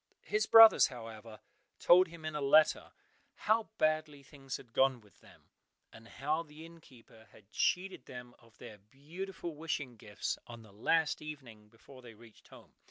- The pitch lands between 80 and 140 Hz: Yes, low, 135 Hz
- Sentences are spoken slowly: No, average, 165 wpm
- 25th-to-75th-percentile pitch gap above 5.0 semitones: Yes, wide, 5.6 semitones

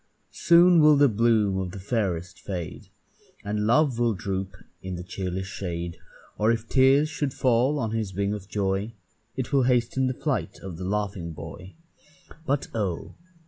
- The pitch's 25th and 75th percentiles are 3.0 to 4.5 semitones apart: No, average, 5.1 semitones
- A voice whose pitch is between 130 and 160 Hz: No, low, 105 Hz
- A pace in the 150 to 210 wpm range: Yes, average, 165 wpm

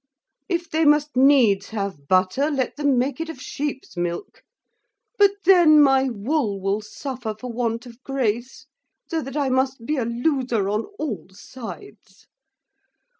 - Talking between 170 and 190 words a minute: No, average, 150 wpm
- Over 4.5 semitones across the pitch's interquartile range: Yes, average, 5.0 semitones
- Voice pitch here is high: Yes, very high, 260 Hz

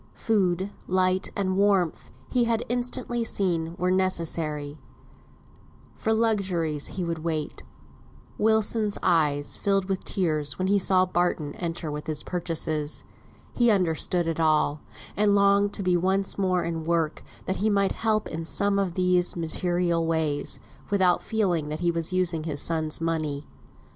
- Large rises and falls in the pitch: No, average, 3.6 semitones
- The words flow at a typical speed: Yes, average, 150 wpm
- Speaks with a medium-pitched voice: Yes, medium, 180 Hz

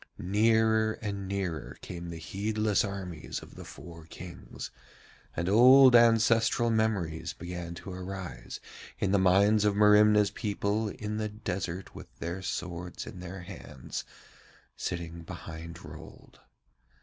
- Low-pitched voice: Yes, very low, 95 Hz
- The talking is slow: Yes, slow, 125 wpm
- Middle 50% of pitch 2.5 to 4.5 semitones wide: Yes, average, 3.7 semitones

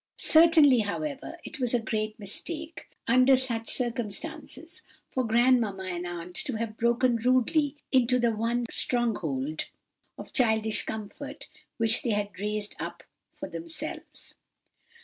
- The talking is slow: Yes, slow, 130 wpm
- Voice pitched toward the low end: No, high, 235 Hz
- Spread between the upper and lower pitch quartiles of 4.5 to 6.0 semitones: No, average, 3.6 semitones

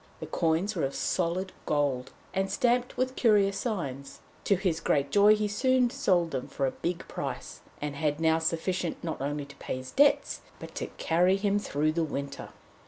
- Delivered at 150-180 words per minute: No, average, 190 wpm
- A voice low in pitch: No, medium, 170 Hz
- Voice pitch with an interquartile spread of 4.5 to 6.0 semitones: Yes, wide, 5.5 semitones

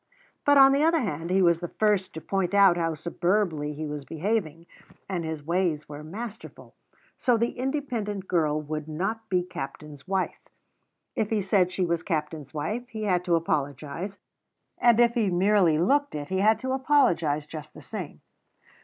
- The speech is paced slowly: No, average, 175 wpm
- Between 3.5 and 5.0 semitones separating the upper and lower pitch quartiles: No, wide, 5.5 semitones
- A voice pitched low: No, medium, 180 Hz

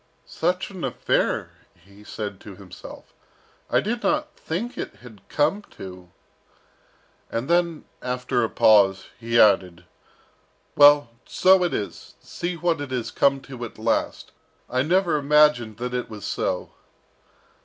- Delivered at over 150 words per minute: No, average, 145 wpm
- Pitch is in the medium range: No, low, 125 Hz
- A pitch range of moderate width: No, wide, 7.6 semitones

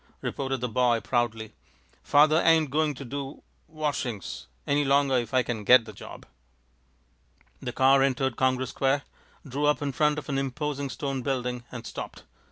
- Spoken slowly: No, average, 165 wpm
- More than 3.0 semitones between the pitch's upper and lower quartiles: No, narrow, 2.6 semitones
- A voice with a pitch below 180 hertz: Yes, low, 135 Hz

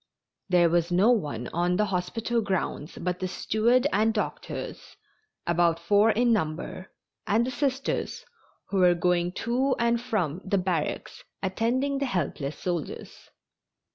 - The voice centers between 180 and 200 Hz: Yes, high, 190 Hz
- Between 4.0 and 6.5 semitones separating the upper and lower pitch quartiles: Yes, average, 5.2 semitones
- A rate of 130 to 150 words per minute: Yes, average, 140 wpm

